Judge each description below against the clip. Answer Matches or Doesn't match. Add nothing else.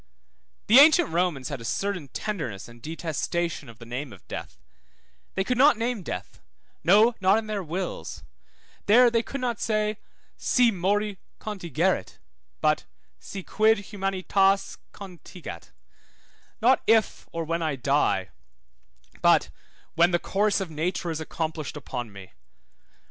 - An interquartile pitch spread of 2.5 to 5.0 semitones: Doesn't match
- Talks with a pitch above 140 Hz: Matches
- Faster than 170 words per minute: Doesn't match